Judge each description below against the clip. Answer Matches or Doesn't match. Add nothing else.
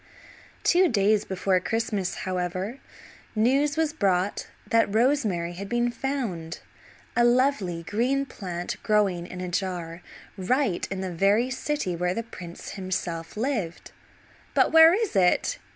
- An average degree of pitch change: Doesn't match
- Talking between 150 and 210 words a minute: Doesn't match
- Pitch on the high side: Matches